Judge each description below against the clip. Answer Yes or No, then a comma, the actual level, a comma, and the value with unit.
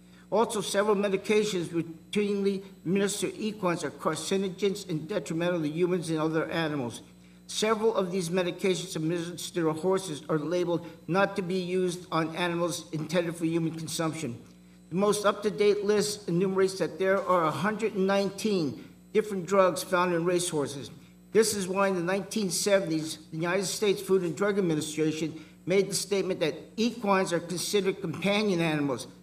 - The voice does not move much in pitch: No, average, 3.4 semitones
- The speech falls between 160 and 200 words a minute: No, average, 150 wpm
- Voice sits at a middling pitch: Yes, medium, 180 Hz